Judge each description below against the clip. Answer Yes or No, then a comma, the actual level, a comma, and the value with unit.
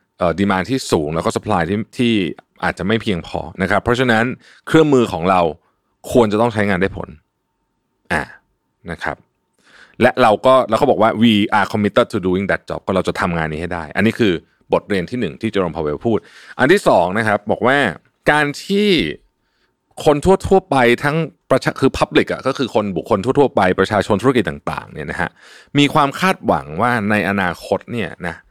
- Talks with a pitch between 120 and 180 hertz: No, low, 110 Hz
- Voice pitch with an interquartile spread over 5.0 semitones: Yes, wide, 5.6 semitones